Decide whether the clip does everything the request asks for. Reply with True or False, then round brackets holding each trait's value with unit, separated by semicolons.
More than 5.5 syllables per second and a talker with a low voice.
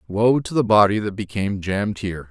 True (6.1 syllables/s; 105 Hz)